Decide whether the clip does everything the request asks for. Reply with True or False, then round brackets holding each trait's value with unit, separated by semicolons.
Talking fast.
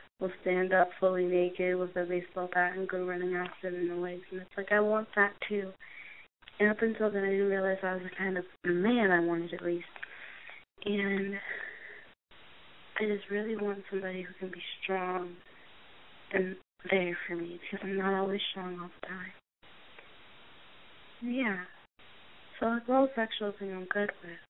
False (175 wpm)